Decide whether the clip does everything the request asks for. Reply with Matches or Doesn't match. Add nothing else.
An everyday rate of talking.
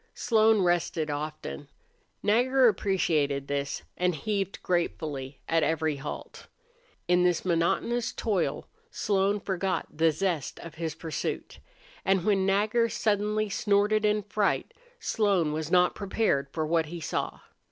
Doesn't match